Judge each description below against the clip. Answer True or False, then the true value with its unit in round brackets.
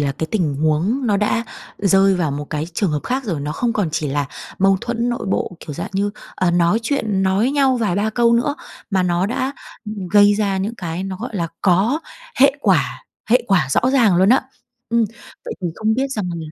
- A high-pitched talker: True (200 Hz)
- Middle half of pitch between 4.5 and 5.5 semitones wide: True (5.1 semitones)